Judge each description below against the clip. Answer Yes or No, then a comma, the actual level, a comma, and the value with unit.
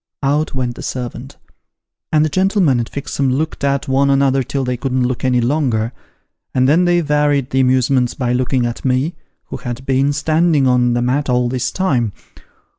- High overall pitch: No, low, 130 Hz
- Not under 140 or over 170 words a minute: No, average, 185 wpm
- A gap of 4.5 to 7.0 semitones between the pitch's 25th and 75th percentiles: No, narrow, 2.5 semitones